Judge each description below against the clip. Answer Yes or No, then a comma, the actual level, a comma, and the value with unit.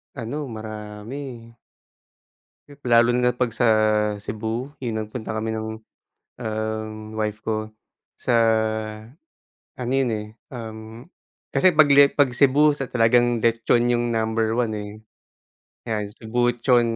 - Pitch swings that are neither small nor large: No, narrow, 2.1 semitones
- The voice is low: Yes, low, 115 Hz